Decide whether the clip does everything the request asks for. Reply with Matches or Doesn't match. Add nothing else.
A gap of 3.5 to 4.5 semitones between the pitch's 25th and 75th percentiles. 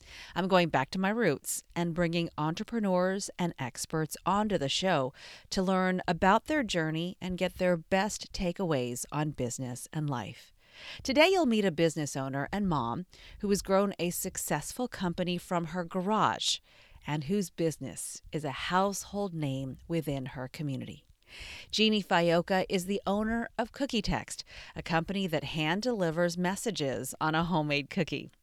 Matches